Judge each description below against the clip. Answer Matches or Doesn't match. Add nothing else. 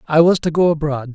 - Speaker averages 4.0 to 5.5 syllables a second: Doesn't match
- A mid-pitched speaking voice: Matches